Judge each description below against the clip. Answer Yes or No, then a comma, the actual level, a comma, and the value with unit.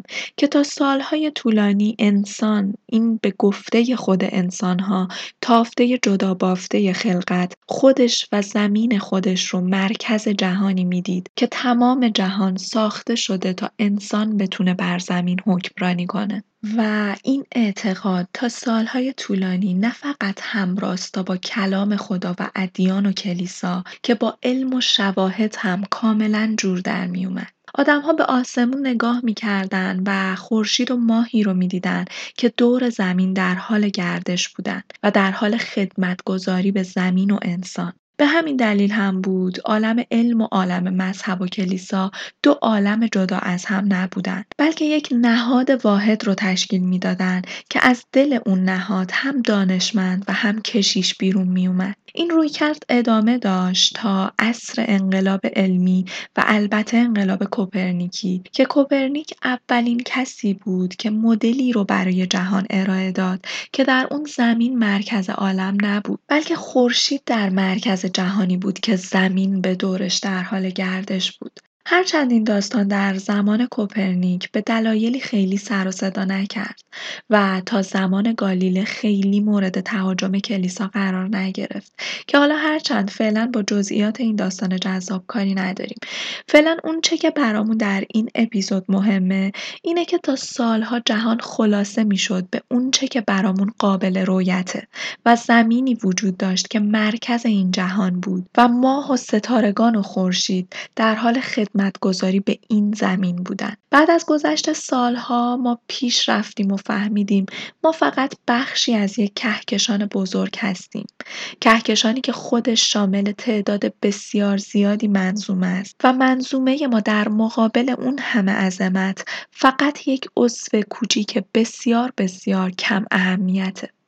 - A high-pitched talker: Yes, high, 210 Hz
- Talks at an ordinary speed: Yes, average, 140 wpm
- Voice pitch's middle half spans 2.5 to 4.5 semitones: Yes, average, 3.8 semitones